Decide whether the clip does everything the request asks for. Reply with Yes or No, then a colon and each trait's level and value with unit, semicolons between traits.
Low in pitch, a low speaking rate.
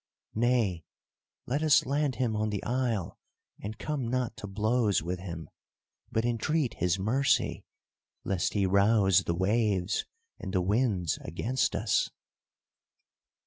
Yes: low, 110 Hz; slow, 130 wpm